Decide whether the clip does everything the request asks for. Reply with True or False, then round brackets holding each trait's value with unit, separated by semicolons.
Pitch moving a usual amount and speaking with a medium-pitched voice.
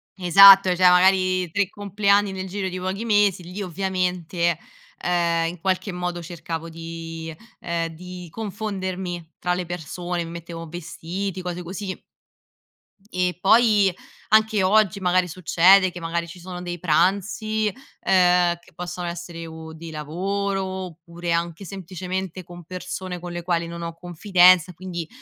False (1.9 semitones; 180 Hz)